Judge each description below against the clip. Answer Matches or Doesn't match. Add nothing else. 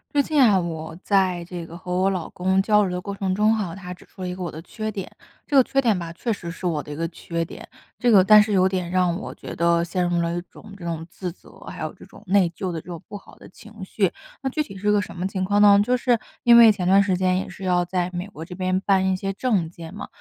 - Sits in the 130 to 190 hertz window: Matches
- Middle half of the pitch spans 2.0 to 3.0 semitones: Matches